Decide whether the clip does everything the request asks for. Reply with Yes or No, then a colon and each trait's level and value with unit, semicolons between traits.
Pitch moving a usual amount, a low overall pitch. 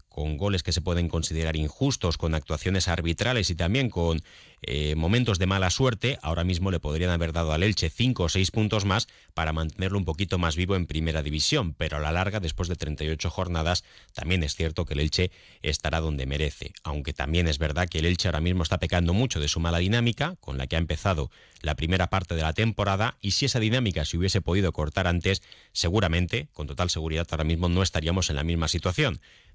Yes: average, 3.3 semitones; very low, 85 Hz